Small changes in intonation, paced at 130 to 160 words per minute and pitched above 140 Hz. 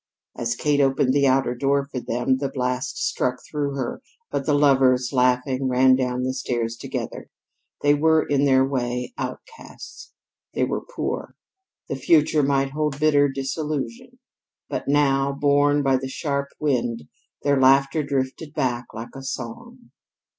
No: narrow, 2.0 semitones; average, 150 wpm; low, 135 Hz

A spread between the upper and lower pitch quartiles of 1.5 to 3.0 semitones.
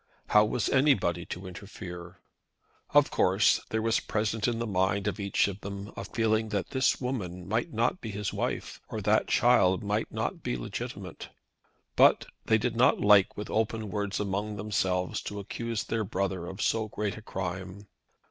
Yes: average, 2.7 semitones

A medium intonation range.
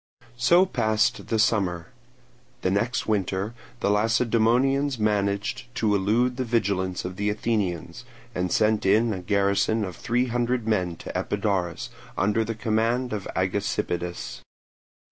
Yes: average, 3.1 semitones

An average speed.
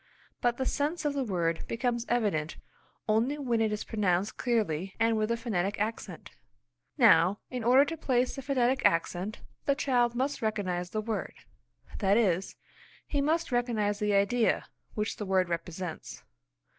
Yes: average, 155 wpm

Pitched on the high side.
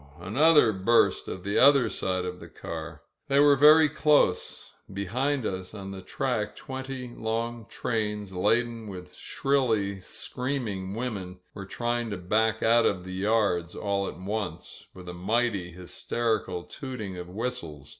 No: low, 105 Hz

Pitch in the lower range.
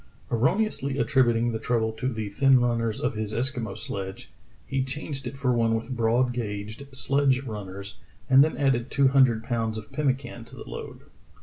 Yes: low, 120 Hz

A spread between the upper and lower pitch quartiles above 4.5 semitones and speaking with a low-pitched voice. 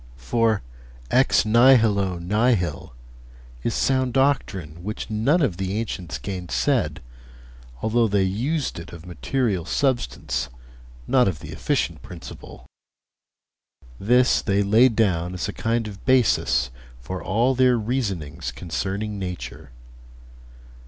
Yes: average, 5.3 semitones; low, 105 Hz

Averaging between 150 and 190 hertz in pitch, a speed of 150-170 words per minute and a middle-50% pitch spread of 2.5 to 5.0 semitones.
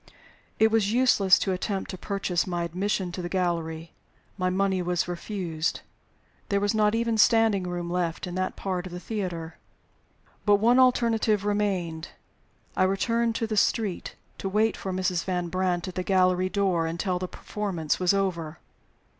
Yes: medium, 185 Hz; average, 165 wpm; average, 2.8 semitones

